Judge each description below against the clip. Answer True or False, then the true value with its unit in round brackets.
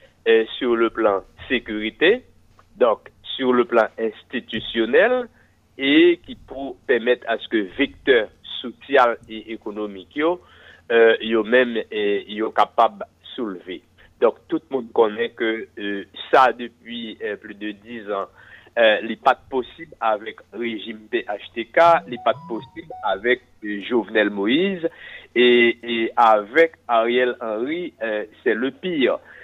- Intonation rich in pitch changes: True (7.0 semitones)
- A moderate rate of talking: False (130 wpm)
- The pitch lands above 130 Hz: False (120 Hz)